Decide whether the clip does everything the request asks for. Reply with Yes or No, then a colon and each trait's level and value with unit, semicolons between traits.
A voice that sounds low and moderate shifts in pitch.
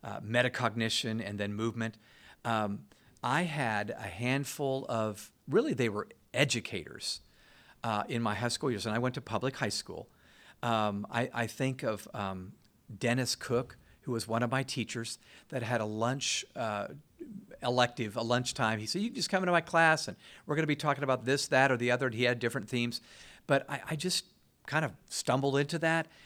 Yes: low, 120 Hz; average, 3.4 semitones